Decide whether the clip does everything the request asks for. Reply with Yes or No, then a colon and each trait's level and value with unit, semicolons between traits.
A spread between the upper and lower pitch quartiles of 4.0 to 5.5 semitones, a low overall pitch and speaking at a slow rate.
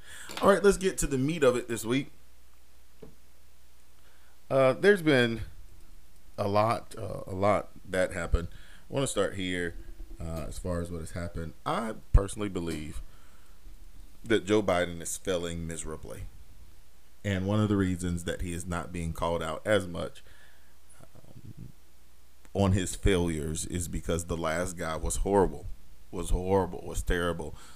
No: average, 4.7 semitones; very low, 85 Hz; average, 155 wpm